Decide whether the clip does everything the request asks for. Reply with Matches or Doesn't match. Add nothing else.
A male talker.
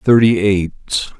Matches